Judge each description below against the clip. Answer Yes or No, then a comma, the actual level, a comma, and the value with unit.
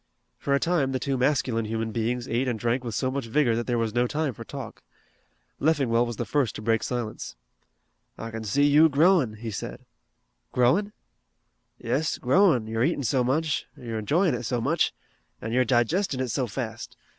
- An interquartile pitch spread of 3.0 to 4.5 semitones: Yes, average, 3.7 semitones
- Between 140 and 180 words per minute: No, average, 190 wpm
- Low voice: Yes, low, 125 Hz